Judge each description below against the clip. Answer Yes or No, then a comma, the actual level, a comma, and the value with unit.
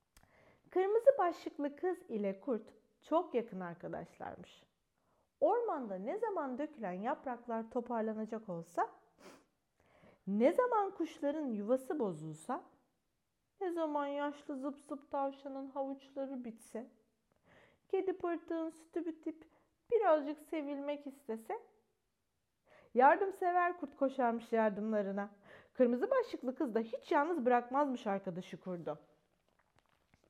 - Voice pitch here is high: Yes, very high, 280 Hz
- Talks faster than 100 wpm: No, slow, 95 wpm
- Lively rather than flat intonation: Yes, wide, 6.6 semitones